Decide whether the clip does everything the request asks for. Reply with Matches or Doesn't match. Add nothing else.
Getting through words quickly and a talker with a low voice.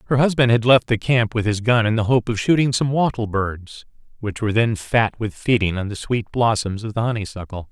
Matches